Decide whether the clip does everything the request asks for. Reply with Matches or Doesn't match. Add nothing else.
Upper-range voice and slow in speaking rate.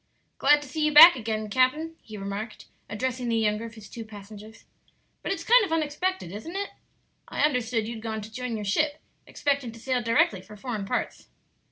Doesn't match